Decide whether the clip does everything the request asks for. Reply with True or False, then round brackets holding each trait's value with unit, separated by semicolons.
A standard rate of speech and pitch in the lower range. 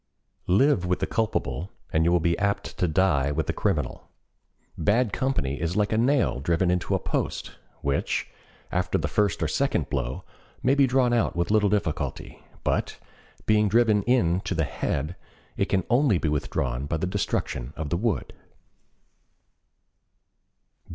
True (160 wpm; 90 Hz)